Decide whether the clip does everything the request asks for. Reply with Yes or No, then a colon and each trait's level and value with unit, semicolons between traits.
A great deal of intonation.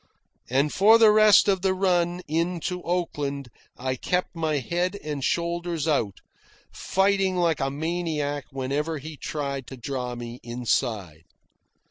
No: average, 4.7 semitones